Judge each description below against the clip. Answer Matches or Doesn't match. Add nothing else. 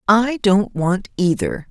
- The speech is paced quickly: Doesn't match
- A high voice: Matches